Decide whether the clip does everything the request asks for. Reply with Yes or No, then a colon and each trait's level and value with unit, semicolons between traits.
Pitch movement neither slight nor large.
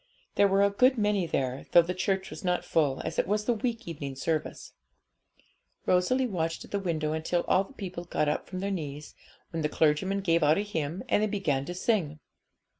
Yes: average, 4.5 semitones